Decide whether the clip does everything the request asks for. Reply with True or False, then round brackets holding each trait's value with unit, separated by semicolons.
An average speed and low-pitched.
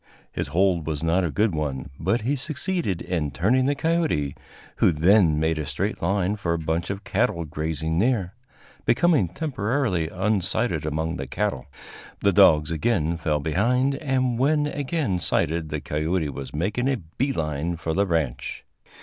True (165 wpm; 90 Hz)